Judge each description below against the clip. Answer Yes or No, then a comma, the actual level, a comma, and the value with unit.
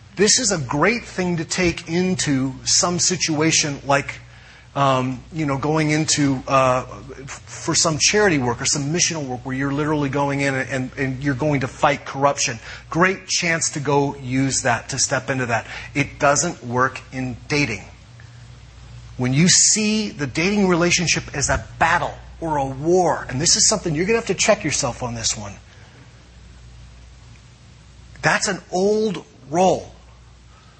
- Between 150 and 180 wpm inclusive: Yes, average, 160 wpm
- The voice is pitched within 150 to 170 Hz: No, medium, 140 Hz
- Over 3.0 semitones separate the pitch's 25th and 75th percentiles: Yes, average, 4.8 semitones